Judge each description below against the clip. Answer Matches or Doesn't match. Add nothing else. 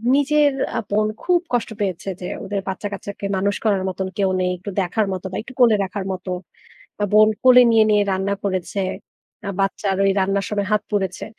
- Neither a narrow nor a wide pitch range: Doesn't match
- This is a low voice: Doesn't match